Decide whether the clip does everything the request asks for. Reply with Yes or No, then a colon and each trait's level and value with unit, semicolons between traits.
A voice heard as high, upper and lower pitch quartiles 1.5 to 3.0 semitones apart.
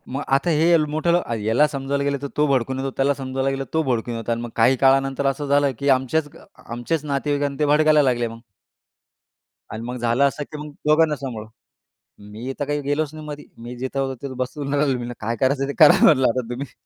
No: low, 135 Hz; average, 2.7 semitones